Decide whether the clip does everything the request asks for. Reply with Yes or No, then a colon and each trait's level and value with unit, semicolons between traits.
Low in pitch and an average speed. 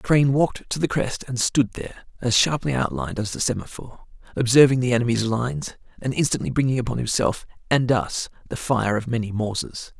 Yes: low, 125 Hz; average, 180 wpm